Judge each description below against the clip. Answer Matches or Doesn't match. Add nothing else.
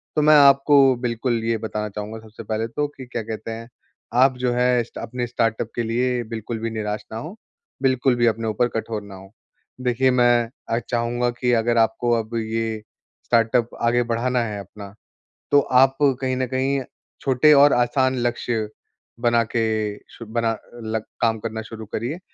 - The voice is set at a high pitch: Doesn't match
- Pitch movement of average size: Doesn't match